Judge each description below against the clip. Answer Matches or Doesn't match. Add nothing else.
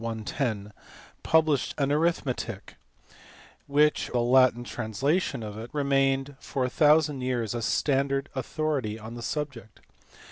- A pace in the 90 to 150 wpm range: Matches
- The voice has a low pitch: Matches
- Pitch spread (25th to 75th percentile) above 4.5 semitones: Doesn't match